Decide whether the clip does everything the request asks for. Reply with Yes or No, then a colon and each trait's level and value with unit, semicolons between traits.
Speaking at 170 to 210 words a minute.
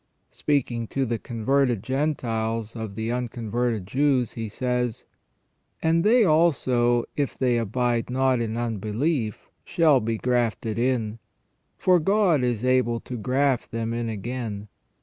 No: average, 140 wpm